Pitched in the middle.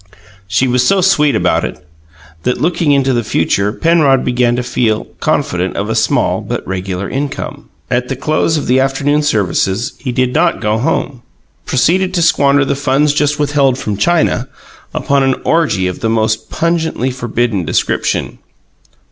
No: low, 130 Hz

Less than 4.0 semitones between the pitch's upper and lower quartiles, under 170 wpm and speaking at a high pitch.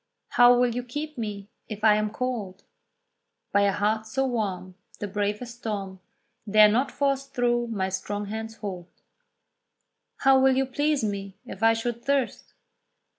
Yes: average, 3.4 semitones; average, 155 wpm; high, 220 Hz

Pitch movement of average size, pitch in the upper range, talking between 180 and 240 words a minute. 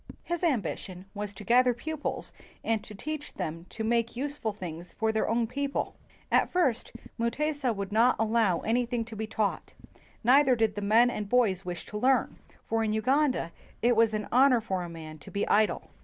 Yes: average, 3.4 semitones; high, 225 Hz; average, 190 wpm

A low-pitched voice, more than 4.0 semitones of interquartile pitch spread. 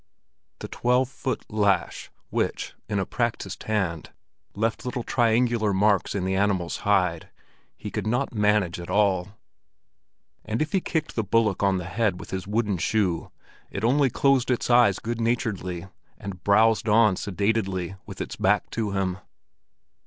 No: low, 105 Hz; average, 3.4 semitones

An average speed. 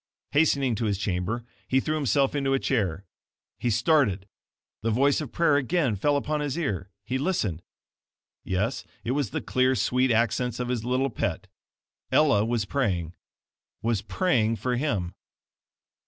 Yes: average, 155 wpm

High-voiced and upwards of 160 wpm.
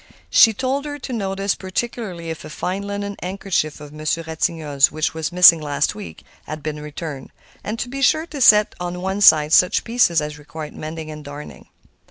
No: medium, 175 Hz; average, 190 wpm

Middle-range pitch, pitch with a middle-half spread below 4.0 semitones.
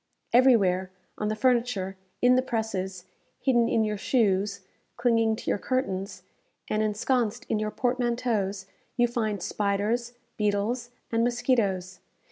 No: high, 220 Hz; average, 3.2 semitones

